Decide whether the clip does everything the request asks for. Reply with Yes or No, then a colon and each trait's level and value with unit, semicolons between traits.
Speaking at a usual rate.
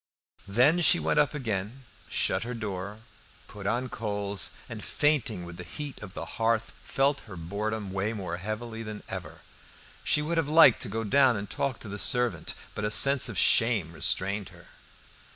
Yes: average, 180 wpm